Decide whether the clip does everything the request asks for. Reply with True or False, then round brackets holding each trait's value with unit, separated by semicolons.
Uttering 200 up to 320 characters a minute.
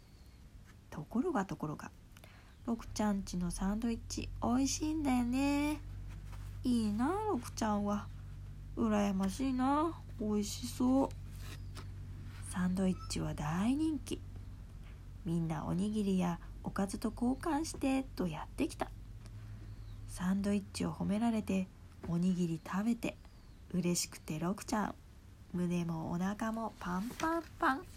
True (260 characters per minute)